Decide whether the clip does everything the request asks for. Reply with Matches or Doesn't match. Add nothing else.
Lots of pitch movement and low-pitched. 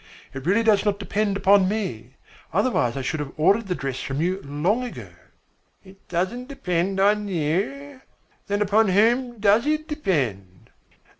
Doesn't match